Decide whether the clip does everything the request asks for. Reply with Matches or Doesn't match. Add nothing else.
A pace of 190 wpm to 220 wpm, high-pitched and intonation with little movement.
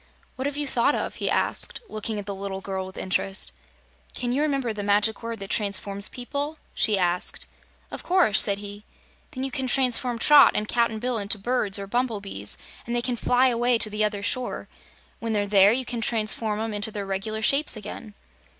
Doesn't match